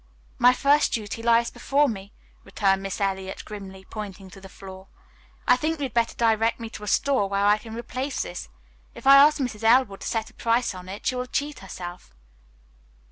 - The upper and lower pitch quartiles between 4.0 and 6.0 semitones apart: Yes, average, 4.4 semitones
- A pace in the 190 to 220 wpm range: Yes, average, 200 wpm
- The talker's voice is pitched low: No, high, 225 Hz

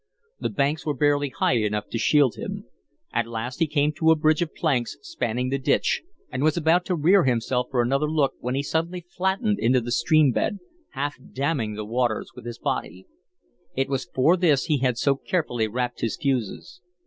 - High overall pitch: No, medium, 140 Hz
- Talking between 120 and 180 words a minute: No, average, 195 wpm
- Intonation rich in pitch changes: No, average, 4.4 semitones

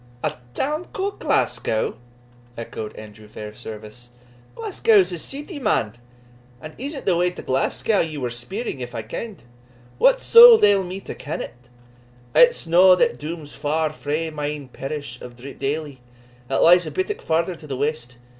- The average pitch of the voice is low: No, medium, 155 Hz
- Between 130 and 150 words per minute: No, average, 160 wpm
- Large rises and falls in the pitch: Yes, wide, 8.3 semitones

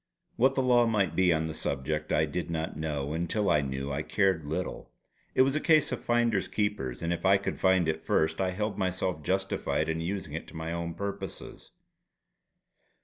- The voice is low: Yes, very low, 85 Hz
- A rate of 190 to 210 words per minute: Yes, average, 200 wpm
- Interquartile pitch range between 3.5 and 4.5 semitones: Yes, average, 4.2 semitones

